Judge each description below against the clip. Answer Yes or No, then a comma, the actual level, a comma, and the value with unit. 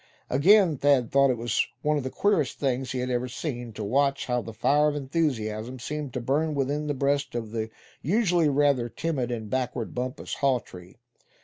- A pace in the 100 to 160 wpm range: No, average, 185 wpm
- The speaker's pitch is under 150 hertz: Yes, low, 135 Hz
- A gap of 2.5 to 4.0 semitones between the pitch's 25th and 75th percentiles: Yes, average, 3.3 semitones